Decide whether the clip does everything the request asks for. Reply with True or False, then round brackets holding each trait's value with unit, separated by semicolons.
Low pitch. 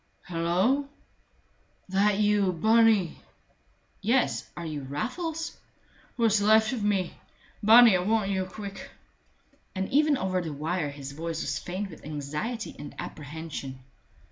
False (190 Hz)